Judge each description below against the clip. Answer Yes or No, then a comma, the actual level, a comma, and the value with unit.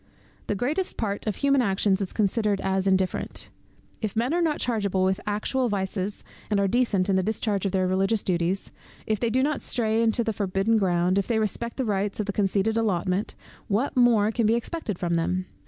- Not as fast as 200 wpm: No, fast, 205 wpm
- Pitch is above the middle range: Yes, high, 205 Hz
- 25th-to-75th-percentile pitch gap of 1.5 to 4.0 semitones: Yes, average, 3.1 semitones